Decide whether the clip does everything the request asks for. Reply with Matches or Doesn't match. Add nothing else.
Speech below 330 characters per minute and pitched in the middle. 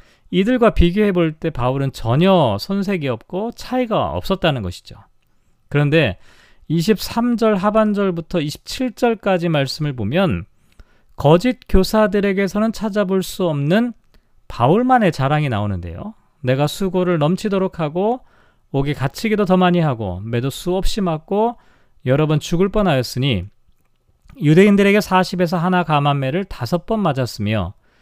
Matches